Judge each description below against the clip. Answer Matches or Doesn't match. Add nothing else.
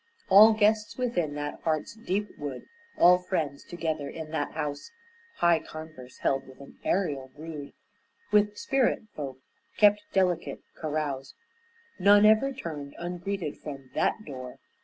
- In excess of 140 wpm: Doesn't match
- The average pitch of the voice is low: Doesn't match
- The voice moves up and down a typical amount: Doesn't match